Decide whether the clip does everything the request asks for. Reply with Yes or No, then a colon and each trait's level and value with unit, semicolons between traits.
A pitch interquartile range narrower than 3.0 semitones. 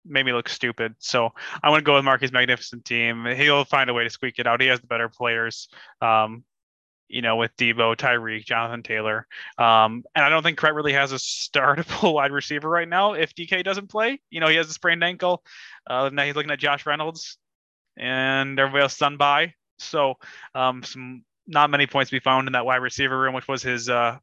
No: average, 3.7 semitones